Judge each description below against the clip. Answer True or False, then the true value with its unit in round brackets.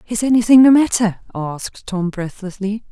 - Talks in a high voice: True (210 Hz)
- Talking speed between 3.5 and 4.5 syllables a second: False (5.1 syllables/s)